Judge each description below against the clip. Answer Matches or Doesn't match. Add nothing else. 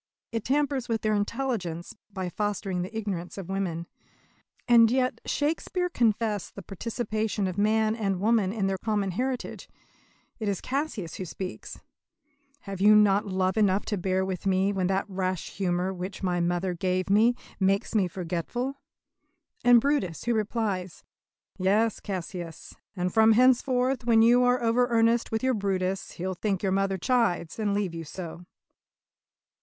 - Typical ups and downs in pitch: Matches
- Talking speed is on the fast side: Doesn't match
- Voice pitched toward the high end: Matches